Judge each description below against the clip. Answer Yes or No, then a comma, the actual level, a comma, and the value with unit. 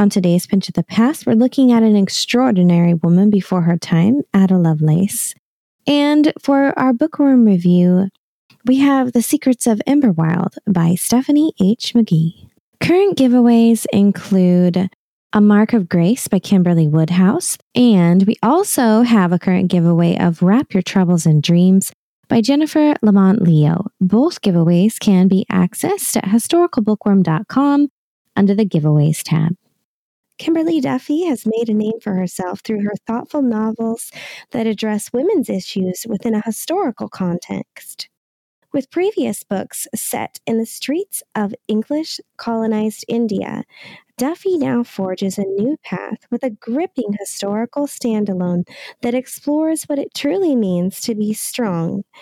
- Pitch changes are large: Yes, wide, 5.9 semitones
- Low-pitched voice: No, high, 220 Hz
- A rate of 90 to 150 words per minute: Yes, average, 140 wpm